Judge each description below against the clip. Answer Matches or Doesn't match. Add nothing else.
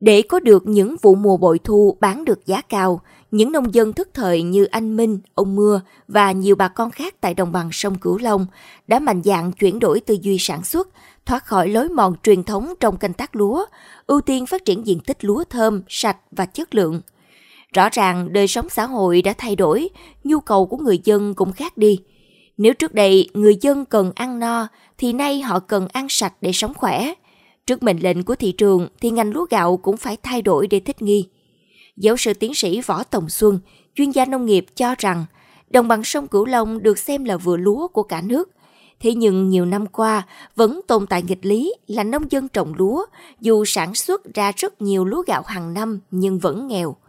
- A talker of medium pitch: Doesn't match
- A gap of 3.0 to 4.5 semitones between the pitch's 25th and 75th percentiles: Matches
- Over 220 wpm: Doesn't match